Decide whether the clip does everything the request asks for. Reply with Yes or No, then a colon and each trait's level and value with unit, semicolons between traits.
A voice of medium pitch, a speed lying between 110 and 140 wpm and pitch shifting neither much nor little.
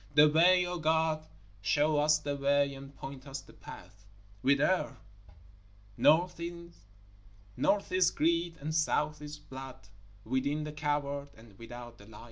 Yes: medium, 145 Hz; slow, 135 wpm; average, 3.3 semitones